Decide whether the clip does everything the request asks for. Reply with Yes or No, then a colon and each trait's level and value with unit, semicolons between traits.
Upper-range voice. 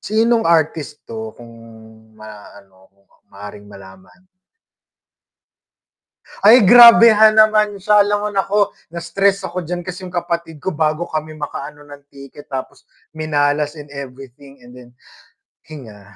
No: medium, 155 Hz